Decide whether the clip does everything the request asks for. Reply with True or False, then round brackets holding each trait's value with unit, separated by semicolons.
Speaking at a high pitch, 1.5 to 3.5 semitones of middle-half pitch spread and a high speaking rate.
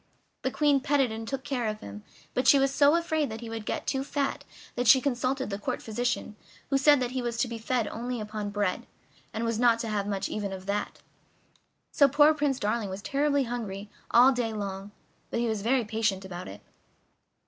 False (235 Hz; 4.2 semitones; 215 wpm)